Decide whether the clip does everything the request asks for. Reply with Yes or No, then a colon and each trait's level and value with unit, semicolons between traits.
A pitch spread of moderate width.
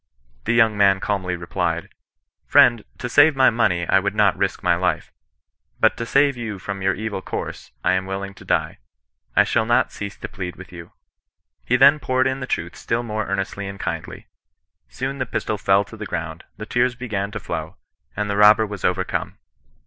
Yes: average, 3.7 semitones